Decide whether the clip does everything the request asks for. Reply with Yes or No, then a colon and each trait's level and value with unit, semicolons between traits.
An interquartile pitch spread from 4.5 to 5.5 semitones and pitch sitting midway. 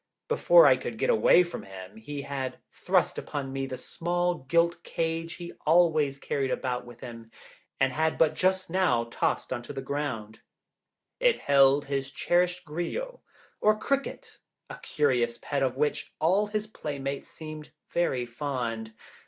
Yes: average, 5.0 semitones; medium, 145 Hz